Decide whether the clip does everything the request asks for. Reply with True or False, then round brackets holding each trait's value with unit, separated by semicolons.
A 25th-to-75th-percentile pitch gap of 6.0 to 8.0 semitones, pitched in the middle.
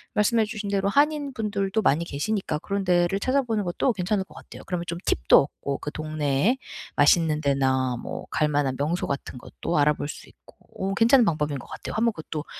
True (6.3 semitones; 175 Hz)